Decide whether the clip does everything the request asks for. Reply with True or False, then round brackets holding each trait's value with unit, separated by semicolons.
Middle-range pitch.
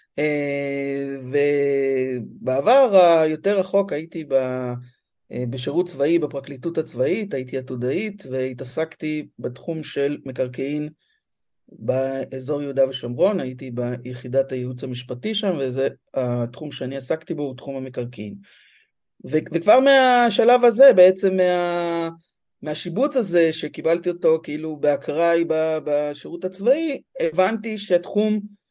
True (150 Hz)